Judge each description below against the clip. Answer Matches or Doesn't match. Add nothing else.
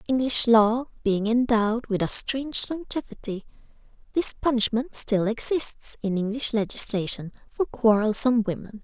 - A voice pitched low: Doesn't match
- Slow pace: Matches